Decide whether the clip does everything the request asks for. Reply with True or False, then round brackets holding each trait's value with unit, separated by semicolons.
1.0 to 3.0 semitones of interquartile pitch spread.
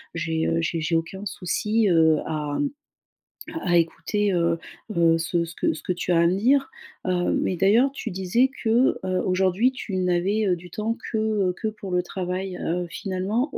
False (3.6 semitones)